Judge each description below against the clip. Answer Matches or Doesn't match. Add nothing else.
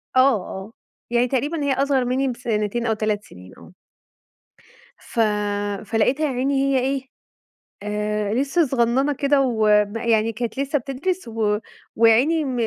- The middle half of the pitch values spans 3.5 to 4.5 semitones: Matches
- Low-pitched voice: Doesn't match